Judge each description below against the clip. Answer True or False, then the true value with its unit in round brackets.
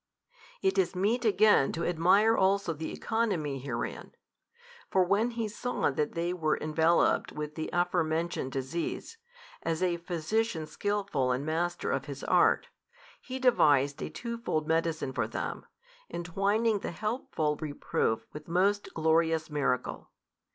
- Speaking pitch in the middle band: True (170 Hz)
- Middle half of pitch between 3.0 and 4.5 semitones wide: False (5.1 semitones)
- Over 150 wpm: False (135 wpm)